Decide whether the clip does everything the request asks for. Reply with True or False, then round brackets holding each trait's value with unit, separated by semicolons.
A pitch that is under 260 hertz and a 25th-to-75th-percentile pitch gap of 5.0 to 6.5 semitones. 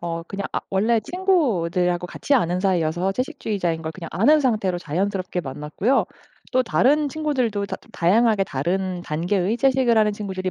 True (195 Hz; 5.4 semitones)